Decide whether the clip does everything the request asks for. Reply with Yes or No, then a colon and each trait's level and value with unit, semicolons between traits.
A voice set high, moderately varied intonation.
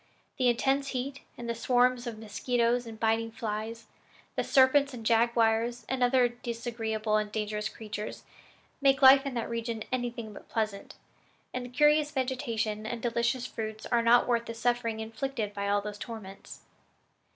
No: high, 235 Hz; narrow, 2.2 semitones